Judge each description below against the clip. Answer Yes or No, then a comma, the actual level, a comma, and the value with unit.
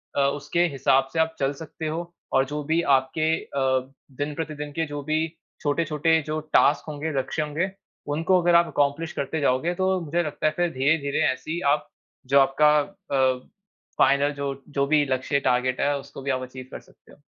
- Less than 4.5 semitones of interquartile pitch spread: Yes, average, 2.8 semitones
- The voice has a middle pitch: Yes, medium, 145 Hz